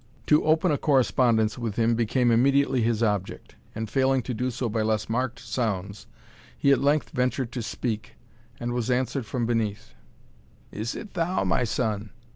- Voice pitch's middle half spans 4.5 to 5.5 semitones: No, average, 2.9 semitones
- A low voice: Yes, low, 120 Hz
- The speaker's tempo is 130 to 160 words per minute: No, average, 170 wpm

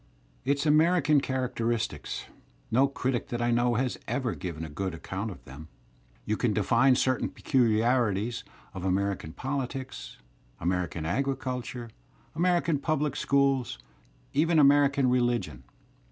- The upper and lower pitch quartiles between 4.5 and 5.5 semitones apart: Yes, average, 4.9 semitones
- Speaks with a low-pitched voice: Yes, low, 125 Hz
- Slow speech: Yes, slow, 125 wpm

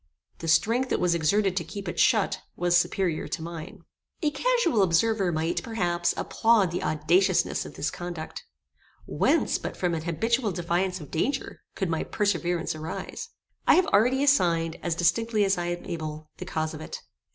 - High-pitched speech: No, medium, 175 Hz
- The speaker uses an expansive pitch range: No, average, 4.4 semitones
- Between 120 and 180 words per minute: Yes, average, 175 wpm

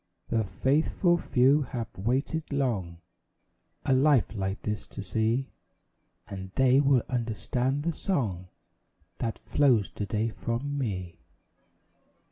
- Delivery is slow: Yes, slow, 115 wpm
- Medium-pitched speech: No, low, 120 Hz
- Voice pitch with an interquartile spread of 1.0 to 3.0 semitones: No, average, 4.9 semitones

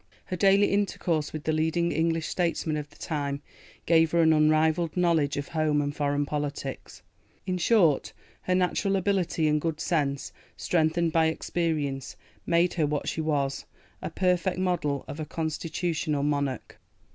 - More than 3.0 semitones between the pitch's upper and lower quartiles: No, average, 2.7 semitones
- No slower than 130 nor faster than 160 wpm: Yes, average, 155 wpm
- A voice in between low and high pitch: Yes, medium, 160 Hz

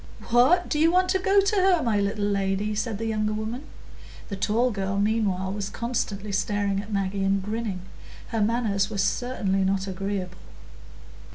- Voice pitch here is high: Yes, high, 210 Hz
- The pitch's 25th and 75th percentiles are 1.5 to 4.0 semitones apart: Yes, average, 3.1 semitones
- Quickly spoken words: No, average, 170 wpm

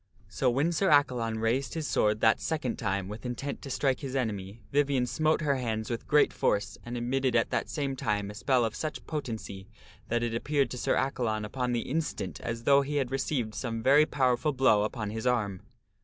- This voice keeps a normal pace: No, fast, 230 wpm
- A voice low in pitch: Yes, low, 125 Hz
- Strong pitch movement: No, average, 3.9 semitones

